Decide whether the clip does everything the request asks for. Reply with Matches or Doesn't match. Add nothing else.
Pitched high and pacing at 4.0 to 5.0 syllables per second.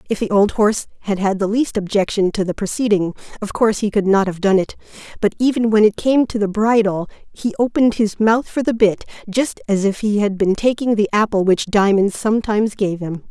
Doesn't match